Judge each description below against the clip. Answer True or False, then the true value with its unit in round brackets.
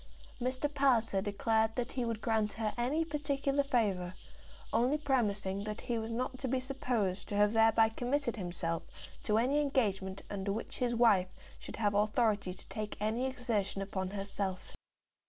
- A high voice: True (225 Hz)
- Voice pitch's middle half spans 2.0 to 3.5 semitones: False (3.9 semitones)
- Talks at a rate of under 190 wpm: True (160 wpm)